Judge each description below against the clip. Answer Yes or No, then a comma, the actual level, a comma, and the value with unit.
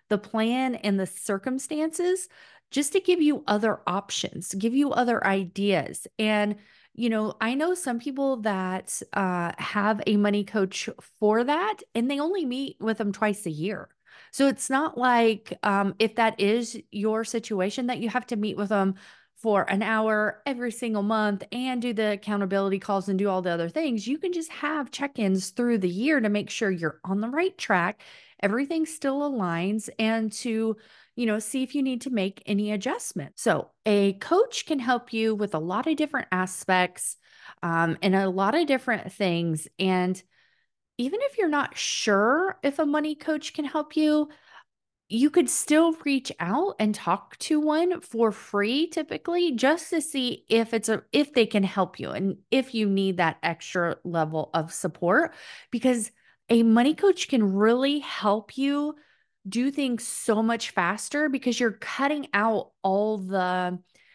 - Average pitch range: No, wide, 5.8 semitones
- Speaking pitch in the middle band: No, high, 225 Hz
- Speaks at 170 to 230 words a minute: Yes, average, 175 wpm